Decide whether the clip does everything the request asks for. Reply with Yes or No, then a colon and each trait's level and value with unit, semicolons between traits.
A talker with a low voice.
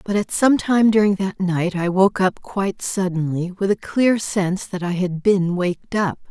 No: high, 190 Hz